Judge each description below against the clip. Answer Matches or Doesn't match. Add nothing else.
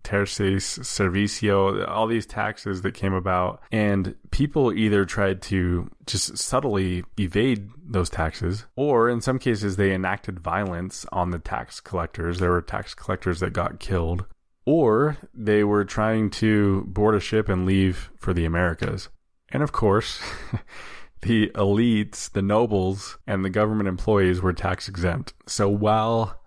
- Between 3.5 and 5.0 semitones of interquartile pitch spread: Doesn't match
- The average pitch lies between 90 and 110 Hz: Matches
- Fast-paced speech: Doesn't match